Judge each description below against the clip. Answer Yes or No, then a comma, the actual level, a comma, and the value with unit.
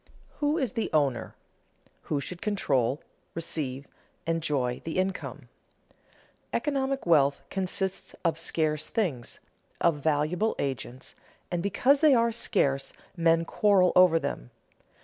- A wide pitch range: Yes, wide, 6.0 semitones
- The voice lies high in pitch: No, medium, 165 Hz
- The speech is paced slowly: Yes, slow, 120 wpm